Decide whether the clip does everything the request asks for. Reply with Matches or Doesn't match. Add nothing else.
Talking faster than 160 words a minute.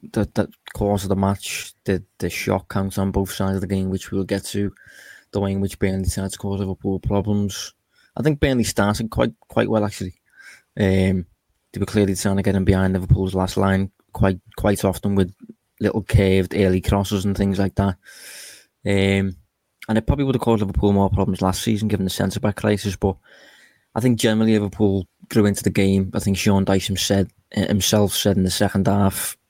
Matches